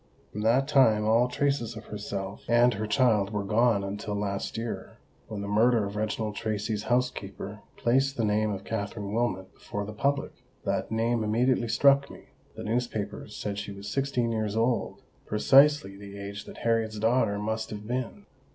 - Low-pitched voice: Yes, low, 110 Hz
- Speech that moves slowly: No, average, 170 wpm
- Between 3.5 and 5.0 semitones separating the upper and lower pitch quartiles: No, average, 2.7 semitones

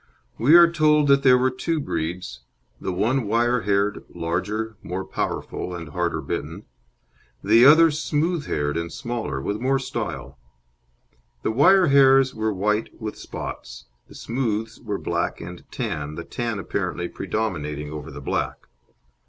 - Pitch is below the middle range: Yes, low, 110 Hz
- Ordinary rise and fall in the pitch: No, wide, 7.4 semitones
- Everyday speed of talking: Yes, average, 145 wpm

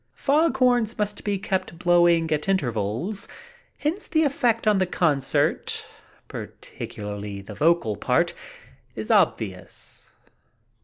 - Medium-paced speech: No, slow, 110 wpm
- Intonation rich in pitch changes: Yes, wide, 8.3 semitones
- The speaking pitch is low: No, medium, 185 Hz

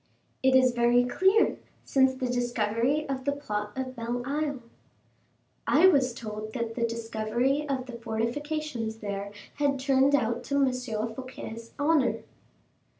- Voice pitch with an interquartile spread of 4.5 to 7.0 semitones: No, average, 3.3 semitones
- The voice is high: Yes, very high, 250 Hz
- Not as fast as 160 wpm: Yes, average, 140 wpm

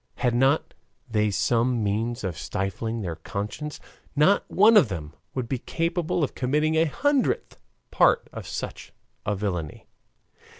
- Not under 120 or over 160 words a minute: Yes, average, 140 wpm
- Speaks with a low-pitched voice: Yes, low, 120 Hz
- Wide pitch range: Yes, wide, 6.9 semitones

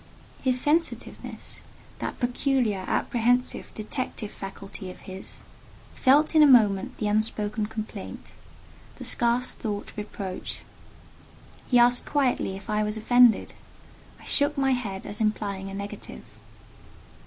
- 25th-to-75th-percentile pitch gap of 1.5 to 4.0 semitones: Yes, average, 3.6 semitones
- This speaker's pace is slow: Yes, slow, 110 wpm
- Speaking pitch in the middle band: No, high, 220 Hz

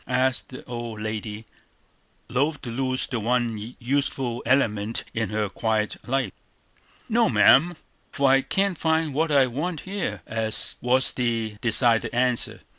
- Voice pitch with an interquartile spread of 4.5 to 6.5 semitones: No, average, 3.3 semitones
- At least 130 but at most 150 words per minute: Yes, slow, 135 wpm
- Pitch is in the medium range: No, low, 125 Hz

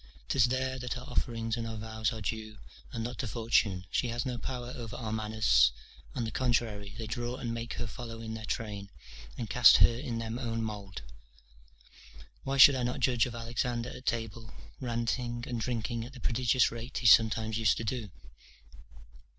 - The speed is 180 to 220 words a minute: Yes, average, 190 wpm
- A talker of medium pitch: No, low, 115 Hz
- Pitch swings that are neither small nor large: No, narrow, 1.8 semitones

